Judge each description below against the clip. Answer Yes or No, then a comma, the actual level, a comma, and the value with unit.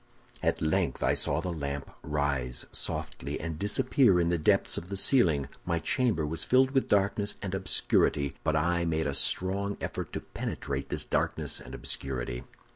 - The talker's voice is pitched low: Yes, very low, 80 Hz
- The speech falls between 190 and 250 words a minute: No, average, 170 wpm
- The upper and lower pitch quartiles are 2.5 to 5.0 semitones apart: No, wide, 5.5 semitones